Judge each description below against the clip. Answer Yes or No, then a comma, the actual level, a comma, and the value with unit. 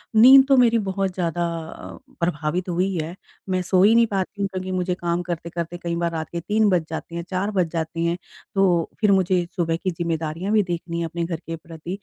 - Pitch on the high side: No, medium, 175 Hz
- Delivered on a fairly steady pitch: Yes, narrow, 2.3 semitones